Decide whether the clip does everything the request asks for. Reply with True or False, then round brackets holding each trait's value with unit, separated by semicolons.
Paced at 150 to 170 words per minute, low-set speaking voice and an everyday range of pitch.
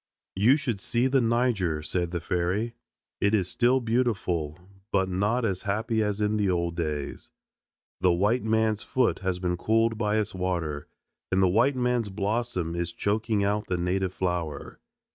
True (165 wpm; 100 Hz; 4.1 semitones)